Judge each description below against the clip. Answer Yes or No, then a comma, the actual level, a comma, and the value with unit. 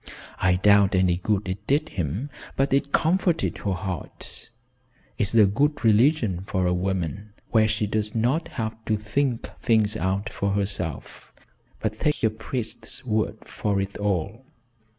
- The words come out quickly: No, average, 150 wpm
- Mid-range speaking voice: No, low, 105 Hz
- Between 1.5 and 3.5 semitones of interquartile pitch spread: Yes, average, 3.0 semitones